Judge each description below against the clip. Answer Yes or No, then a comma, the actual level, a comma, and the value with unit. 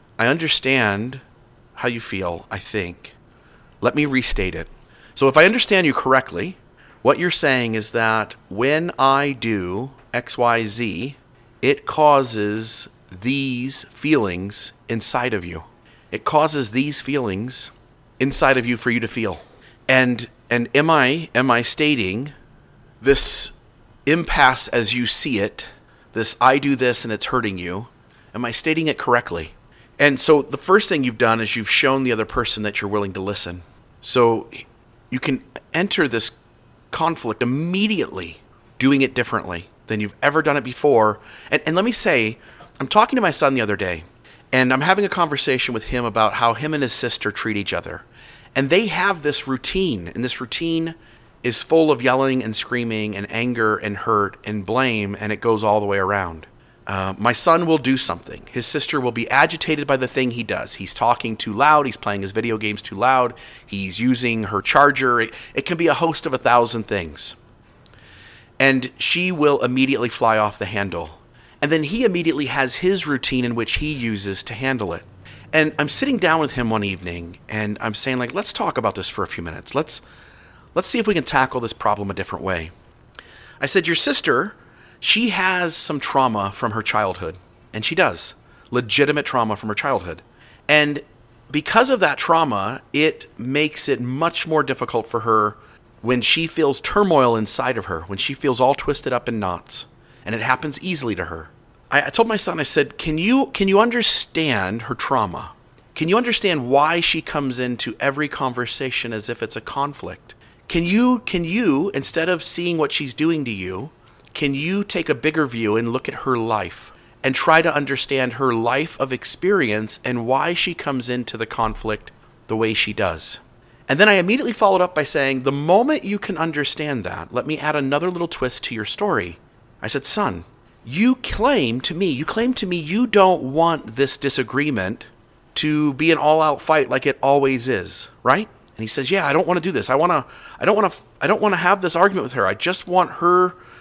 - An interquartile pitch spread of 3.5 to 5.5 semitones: Yes, average, 5.2 semitones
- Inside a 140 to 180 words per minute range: No, average, 190 wpm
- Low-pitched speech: Yes, low, 130 Hz